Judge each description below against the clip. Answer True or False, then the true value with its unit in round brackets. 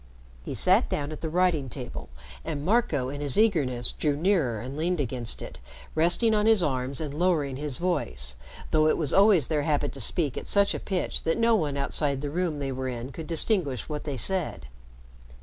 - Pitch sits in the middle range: True (150 Hz)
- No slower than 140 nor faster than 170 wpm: False (200 wpm)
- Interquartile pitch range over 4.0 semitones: True (4.7 semitones)